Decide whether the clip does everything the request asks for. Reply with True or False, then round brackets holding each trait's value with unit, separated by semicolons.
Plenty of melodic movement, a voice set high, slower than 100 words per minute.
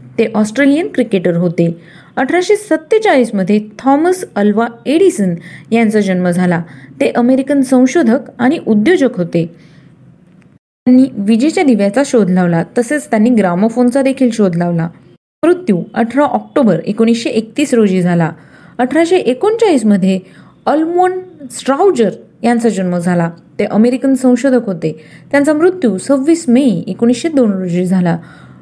False (7.1 semitones; 230 Hz; 115 wpm)